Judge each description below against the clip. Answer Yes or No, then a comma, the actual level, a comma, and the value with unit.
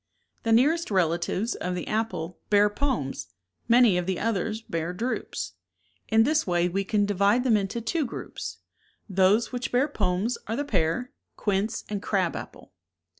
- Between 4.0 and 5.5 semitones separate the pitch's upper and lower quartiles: Yes, average, 4.4 semitones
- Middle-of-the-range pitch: No, high, 210 Hz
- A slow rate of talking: No, average, 160 wpm